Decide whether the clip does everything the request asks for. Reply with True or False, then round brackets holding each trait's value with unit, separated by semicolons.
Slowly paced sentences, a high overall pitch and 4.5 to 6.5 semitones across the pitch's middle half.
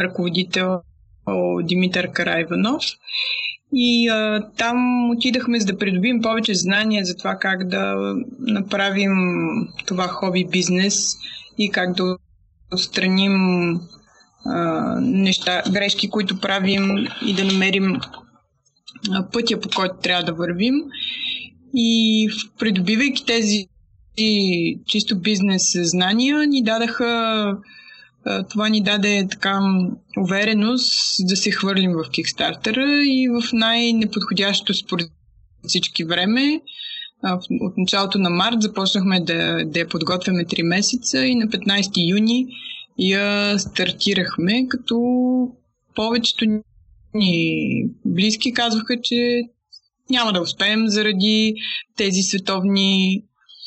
False (105 wpm; 205 Hz; 3.9 semitones)